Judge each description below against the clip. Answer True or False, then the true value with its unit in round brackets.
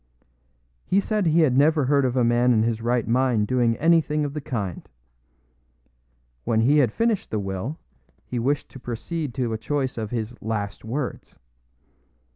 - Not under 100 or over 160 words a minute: False (170 wpm)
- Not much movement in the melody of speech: False (4.5 semitones)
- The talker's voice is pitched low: True (125 Hz)